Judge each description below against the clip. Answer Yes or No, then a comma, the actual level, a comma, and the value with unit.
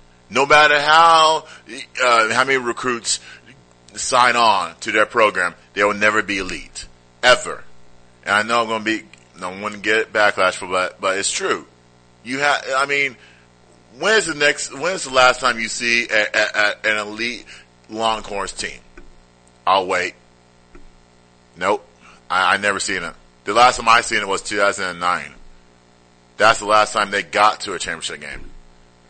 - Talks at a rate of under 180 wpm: Yes, average, 170 wpm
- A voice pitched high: No, very low, 95 Hz